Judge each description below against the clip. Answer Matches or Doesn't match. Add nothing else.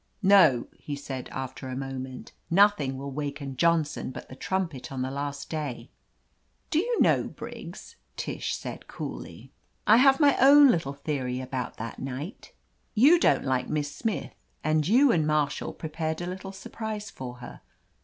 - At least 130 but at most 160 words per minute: Doesn't match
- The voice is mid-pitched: Matches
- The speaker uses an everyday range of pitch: Doesn't match